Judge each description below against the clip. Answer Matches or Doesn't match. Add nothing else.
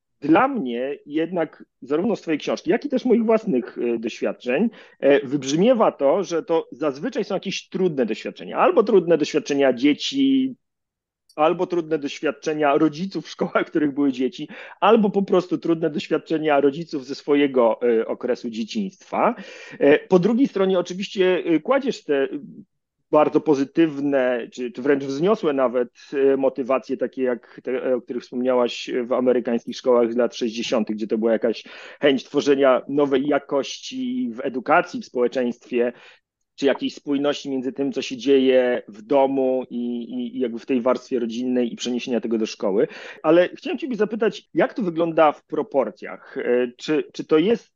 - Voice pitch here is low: Doesn't match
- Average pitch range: Doesn't match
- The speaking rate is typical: Matches